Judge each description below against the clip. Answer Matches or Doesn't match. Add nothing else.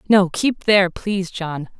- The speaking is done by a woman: Matches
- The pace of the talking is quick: Doesn't match